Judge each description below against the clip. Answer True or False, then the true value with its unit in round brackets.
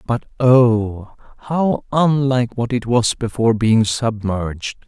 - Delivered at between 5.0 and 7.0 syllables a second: False (3.9 syllables/s)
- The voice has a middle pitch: False (120 Hz)